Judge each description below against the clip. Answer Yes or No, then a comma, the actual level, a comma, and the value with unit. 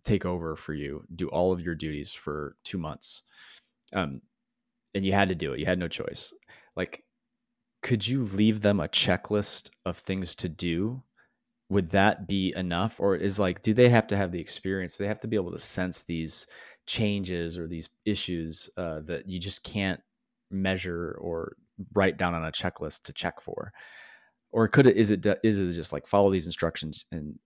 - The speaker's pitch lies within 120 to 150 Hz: No, very low, 95 Hz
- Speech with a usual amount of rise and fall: Yes, average, 3.9 semitones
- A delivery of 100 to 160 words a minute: No, average, 195 wpm